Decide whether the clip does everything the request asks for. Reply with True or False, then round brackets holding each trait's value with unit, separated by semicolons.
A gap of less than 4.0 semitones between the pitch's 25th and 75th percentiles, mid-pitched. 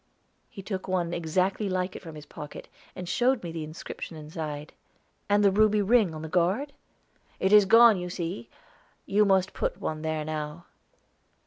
False (4.3 semitones; 180 Hz)